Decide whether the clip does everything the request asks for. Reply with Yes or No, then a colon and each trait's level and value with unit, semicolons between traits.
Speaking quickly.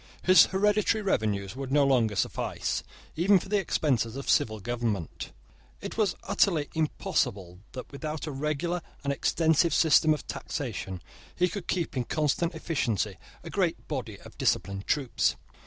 No: average, 150 wpm